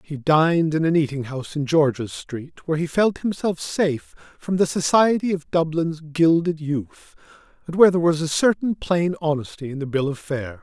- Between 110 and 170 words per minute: No, average, 190 wpm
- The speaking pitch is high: No, medium, 160 Hz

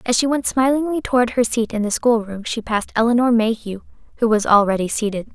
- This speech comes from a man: No, female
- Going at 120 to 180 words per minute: No, average, 200 wpm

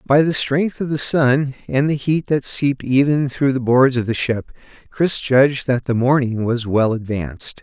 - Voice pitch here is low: Yes, low, 130 Hz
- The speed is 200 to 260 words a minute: Yes, fast, 205 wpm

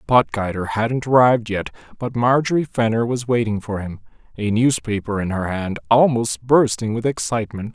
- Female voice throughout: No, male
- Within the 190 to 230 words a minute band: No, average, 155 wpm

